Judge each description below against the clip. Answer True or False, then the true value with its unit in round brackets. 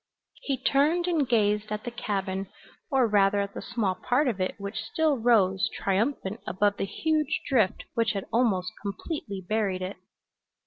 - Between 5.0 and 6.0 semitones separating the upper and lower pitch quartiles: False (4.6 semitones)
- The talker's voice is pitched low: False (215 Hz)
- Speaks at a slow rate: False (165 wpm)